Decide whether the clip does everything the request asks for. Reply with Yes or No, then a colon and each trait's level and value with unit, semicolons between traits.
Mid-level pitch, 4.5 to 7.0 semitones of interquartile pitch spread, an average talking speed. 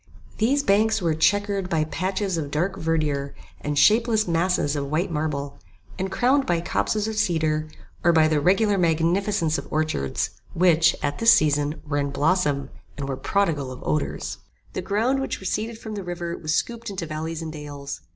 Yes: medium, 165 Hz; average, 4.8 semitones; average, 175 wpm